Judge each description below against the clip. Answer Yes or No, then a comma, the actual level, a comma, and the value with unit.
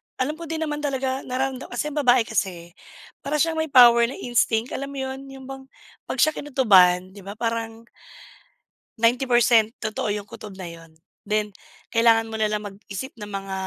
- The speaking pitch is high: Yes, high, 235 Hz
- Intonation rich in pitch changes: No, average, 4.3 semitones